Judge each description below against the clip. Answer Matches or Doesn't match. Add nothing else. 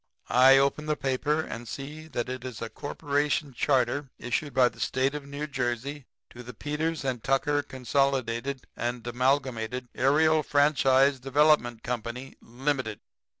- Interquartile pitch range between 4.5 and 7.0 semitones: Doesn't match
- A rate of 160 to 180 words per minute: Doesn't match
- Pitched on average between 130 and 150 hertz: Matches